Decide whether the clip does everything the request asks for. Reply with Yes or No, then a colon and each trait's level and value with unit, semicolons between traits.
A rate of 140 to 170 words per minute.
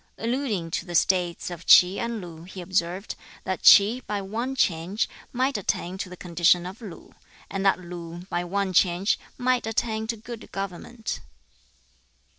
Yes: average, 160 wpm